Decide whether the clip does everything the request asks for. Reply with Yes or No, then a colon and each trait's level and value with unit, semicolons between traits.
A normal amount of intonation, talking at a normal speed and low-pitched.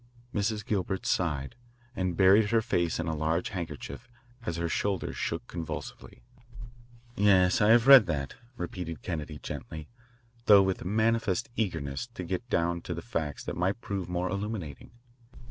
Yes: average, 3.9 semitones; average, 145 wpm; very low, 90 Hz